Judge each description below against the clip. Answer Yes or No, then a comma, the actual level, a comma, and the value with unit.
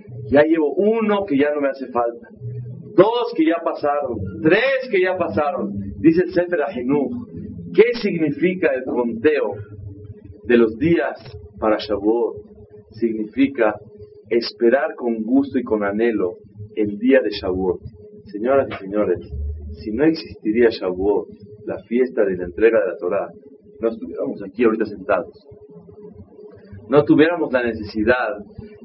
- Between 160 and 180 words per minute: No, average, 135 wpm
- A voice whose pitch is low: Yes, low, 120 Hz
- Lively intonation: Yes, wide, 7.1 semitones